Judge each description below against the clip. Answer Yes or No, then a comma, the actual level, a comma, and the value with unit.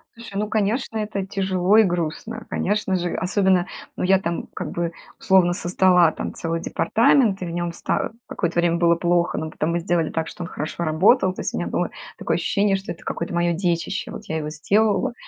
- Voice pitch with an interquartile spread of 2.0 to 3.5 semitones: Yes, average, 2.7 semitones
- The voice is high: No, medium, 180 Hz